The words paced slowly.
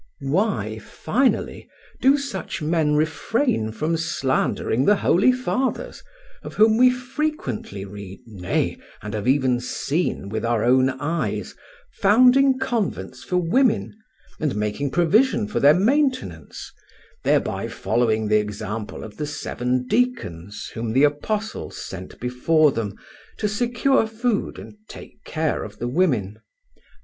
Yes: slow, 130 wpm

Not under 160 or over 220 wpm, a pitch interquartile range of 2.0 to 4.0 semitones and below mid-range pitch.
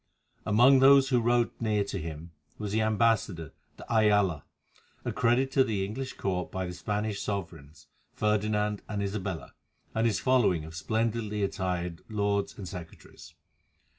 No: average, 140 wpm; average, 3.6 semitones; low, 105 Hz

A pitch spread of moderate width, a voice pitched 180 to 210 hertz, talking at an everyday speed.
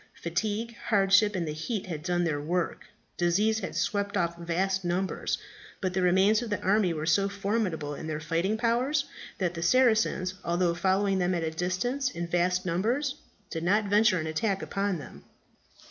Yes: average, 3.5 semitones; medium, 185 Hz; average, 175 wpm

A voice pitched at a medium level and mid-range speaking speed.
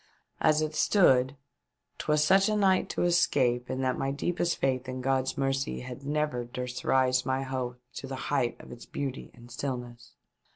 No: low, 130 Hz; average, 175 wpm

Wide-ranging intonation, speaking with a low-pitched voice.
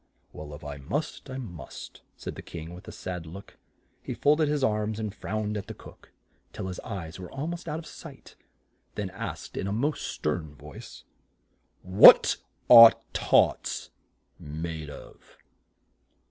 Yes: wide, 7.0 semitones; very low, 95 Hz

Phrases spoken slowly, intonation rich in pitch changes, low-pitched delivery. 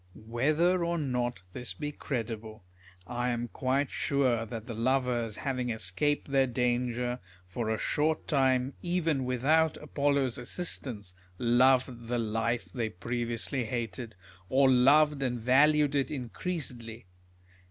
No: slow, 130 wpm; average, 3.2 semitones; low, 125 Hz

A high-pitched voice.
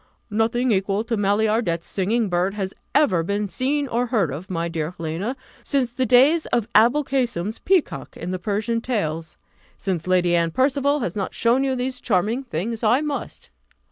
Yes: high, 220 Hz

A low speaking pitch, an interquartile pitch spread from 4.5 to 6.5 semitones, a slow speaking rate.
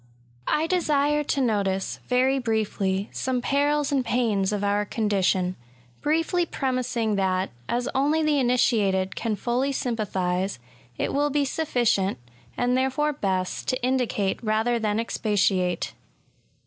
No: high, 235 Hz; wide, 5.4 semitones; slow, 130 wpm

